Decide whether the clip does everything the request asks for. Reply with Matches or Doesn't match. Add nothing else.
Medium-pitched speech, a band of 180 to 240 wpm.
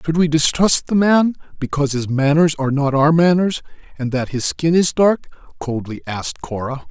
Matches